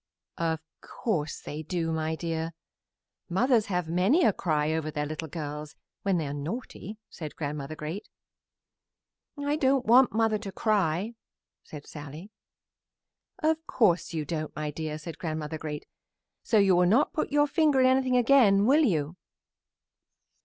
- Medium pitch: Yes, medium, 175 Hz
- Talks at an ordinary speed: Yes, average, 150 wpm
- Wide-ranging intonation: Yes, wide, 6.8 semitones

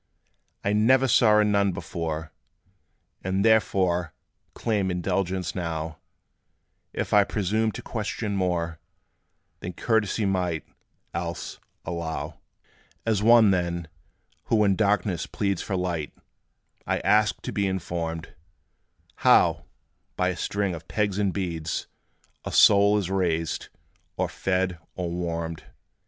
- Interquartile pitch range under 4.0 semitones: Yes, average, 3.3 semitones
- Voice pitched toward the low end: Yes, very low, 95 Hz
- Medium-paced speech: No, slow, 120 wpm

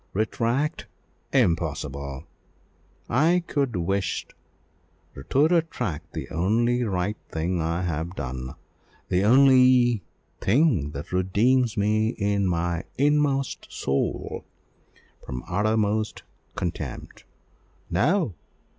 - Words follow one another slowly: Yes, slow, 90 wpm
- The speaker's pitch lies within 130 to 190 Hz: No, low, 105 Hz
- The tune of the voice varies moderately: No, wide, 7.0 semitones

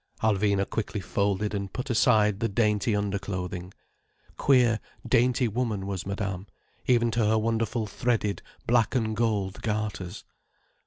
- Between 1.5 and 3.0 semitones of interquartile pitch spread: Yes, narrow, 2.5 semitones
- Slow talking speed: Yes, slow, 125 wpm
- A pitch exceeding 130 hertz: No, low, 105 Hz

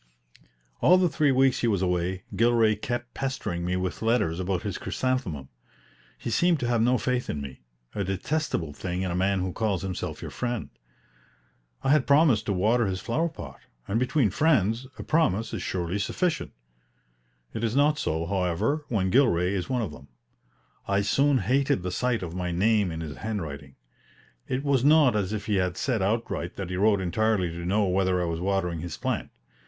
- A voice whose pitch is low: Yes, low, 105 Hz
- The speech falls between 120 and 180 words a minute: No, average, 190 wpm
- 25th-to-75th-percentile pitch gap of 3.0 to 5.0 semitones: No, wide, 5.6 semitones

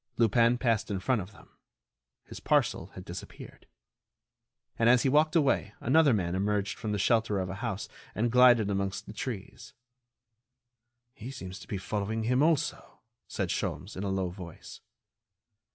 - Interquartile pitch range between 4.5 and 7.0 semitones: No, average, 4.1 semitones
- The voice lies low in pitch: Yes, low, 110 Hz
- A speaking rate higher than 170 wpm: No, average, 160 wpm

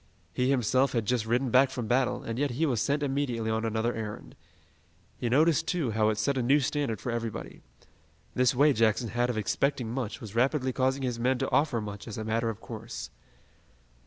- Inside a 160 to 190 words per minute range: No, fast, 205 wpm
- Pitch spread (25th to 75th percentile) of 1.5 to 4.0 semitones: Yes, average, 3.2 semitones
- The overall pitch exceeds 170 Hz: No, low, 120 Hz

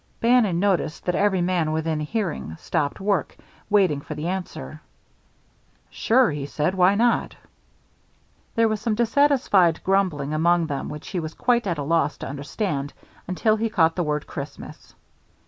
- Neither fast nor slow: Yes, average, 155 wpm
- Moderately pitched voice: Yes, medium, 180 Hz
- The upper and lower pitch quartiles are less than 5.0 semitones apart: No, wide, 5.4 semitones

